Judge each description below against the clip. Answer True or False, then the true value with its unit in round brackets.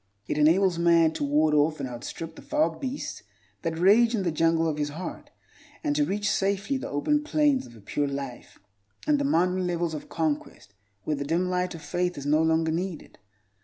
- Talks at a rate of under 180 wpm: False (200 wpm)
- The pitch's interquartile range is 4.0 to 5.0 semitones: True (4.5 semitones)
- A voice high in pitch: False (165 Hz)